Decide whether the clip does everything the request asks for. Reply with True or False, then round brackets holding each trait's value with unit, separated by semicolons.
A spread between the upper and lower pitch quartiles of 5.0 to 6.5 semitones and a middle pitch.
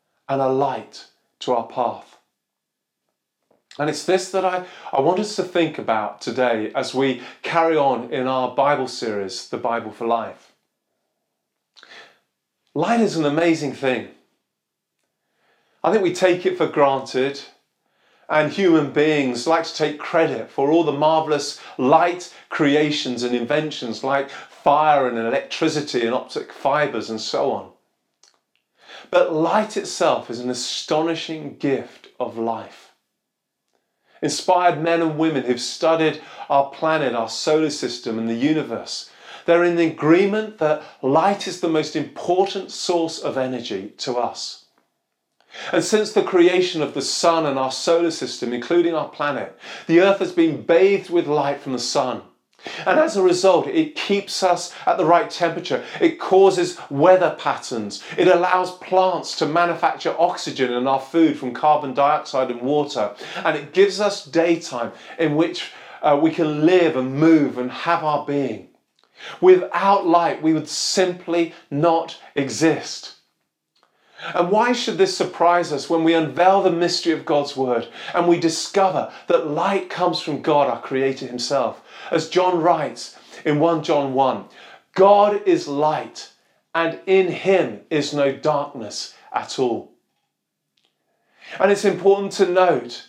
False (4.3 semitones; 160 Hz)